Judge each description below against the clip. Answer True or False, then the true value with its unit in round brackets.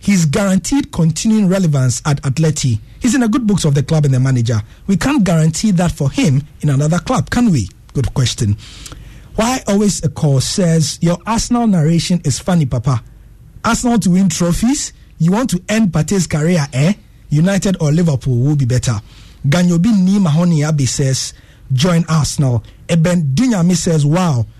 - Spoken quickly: False (165 wpm)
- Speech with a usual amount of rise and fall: False (6.0 semitones)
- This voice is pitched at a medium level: True (160 Hz)